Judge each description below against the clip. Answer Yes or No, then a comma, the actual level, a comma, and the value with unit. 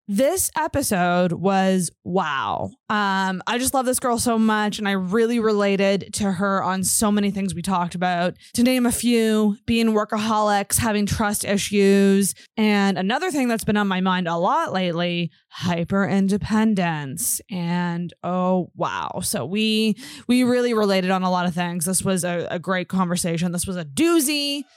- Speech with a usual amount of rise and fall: Yes, average, 3.3 semitones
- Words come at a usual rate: Yes, average, 170 wpm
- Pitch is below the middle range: No, high, 195 Hz